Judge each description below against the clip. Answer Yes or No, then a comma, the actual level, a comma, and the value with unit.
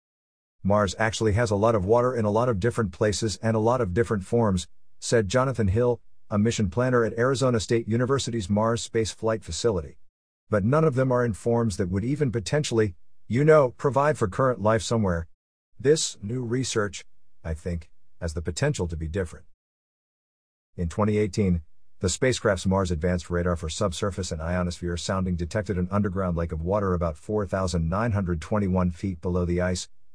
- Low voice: Yes, low, 105 Hz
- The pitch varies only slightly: No, average, 4.8 semitones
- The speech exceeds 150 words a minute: Yes, average, 170 wpm